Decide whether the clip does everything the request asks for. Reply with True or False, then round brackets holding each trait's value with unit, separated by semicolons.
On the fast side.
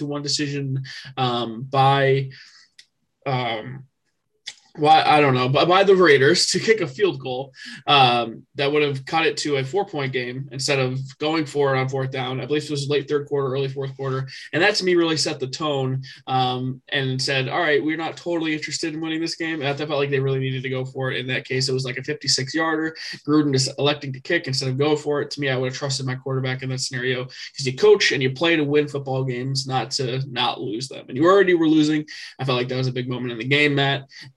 True (250 wpm)